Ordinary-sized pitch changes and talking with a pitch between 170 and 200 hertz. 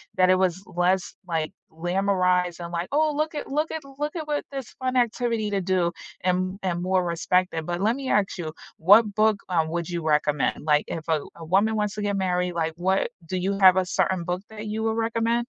Yes: average, 3.9 semitones; medium, 185 Hz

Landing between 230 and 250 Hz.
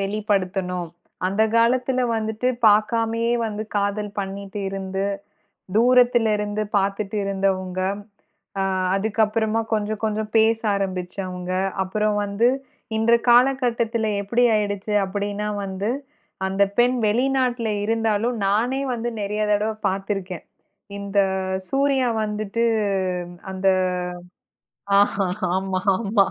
No: high, 210 Hz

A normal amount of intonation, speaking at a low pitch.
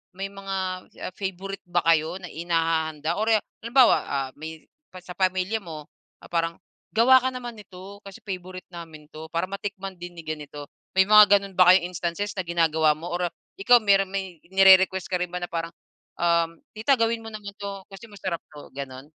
No: average, 3.0 semitones; medium, 185 Hz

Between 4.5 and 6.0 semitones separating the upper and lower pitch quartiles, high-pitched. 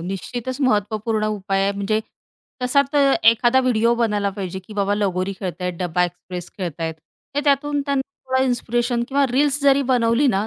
Yes: average, 5.0 semitones; high, 225 Hz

